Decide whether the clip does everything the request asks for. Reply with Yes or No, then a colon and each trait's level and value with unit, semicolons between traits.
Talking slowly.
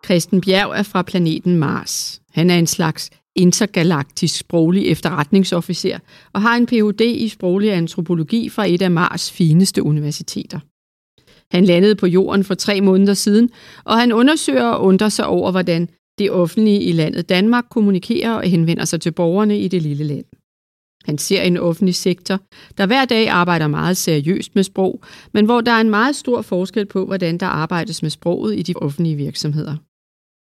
No: average, 175 wpm